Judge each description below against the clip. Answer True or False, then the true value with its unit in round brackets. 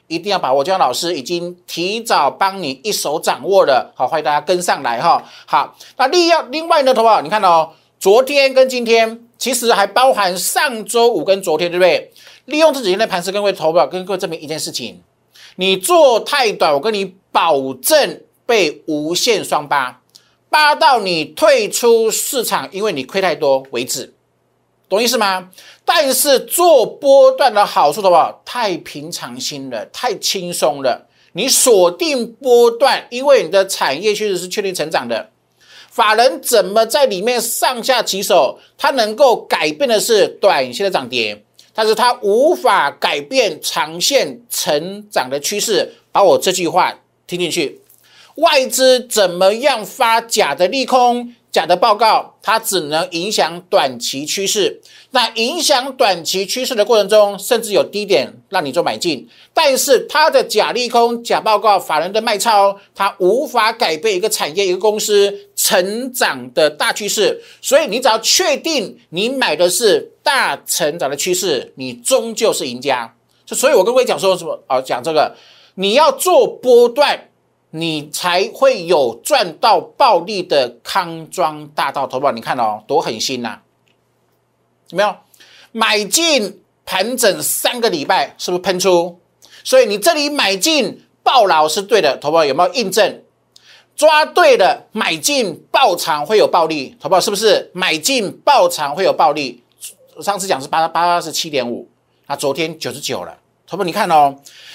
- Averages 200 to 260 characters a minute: True (240 characters per minute)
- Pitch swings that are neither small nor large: False (8.2 semitones)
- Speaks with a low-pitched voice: False (215 Hz)